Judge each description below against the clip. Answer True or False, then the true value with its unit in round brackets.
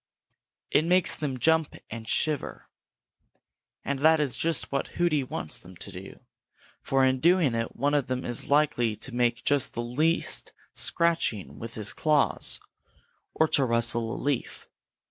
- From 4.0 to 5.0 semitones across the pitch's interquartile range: True (4.7 semitones)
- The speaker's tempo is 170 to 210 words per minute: False (155 wpm)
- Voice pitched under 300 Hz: True (135 Hz)